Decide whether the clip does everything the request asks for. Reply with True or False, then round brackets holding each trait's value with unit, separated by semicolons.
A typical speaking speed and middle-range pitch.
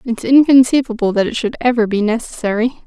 False (170 wpm; 235 Hz)